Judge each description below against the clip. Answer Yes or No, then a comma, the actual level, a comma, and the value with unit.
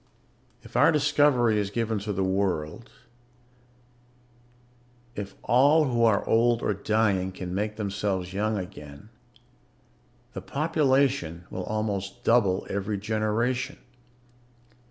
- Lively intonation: No, average, 3.7 semitones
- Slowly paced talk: Yes, slow, 110 wpm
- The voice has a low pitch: Yes, low, 105 Hz